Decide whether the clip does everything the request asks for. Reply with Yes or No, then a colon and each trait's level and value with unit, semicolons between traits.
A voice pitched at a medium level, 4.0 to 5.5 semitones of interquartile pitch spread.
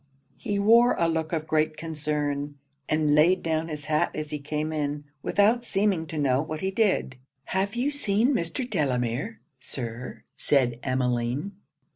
Yes: medium, 155 Hz; average, 5.2 semitones